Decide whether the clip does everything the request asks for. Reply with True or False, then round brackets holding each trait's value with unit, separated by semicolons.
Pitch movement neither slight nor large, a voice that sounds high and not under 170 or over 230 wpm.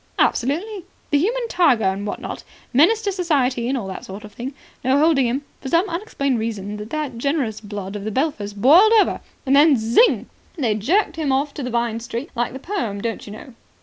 False (6.3 semitones; 265 Hz; 205 wpm)